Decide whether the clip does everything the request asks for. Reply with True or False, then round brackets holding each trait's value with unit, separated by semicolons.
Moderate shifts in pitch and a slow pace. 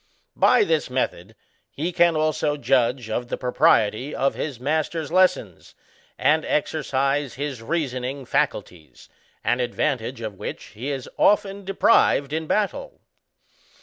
True (4.5 semitones; 125 wpm)